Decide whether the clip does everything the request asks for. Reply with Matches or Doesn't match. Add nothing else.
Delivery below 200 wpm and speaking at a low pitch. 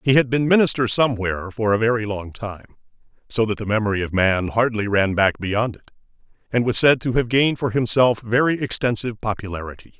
Matches